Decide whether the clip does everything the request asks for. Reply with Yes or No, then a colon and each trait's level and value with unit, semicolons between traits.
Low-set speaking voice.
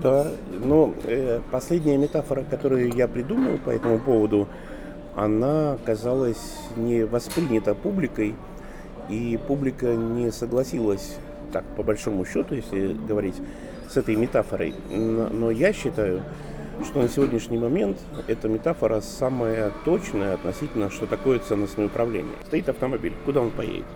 Yes: low, 115 Hz